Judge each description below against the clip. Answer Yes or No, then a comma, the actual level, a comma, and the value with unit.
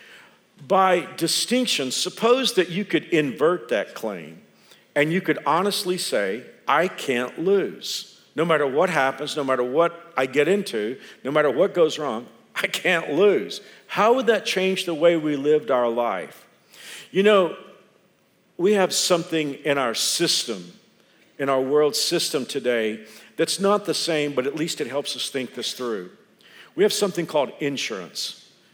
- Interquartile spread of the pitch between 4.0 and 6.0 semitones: Yes, average, 5.1 semitones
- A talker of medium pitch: Yes, medium, 165 Hz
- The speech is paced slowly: No, average, 160 wpm